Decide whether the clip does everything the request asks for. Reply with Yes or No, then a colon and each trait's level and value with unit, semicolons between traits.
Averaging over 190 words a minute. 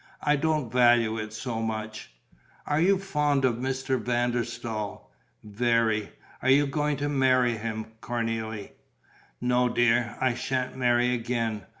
No: average, 140 wpm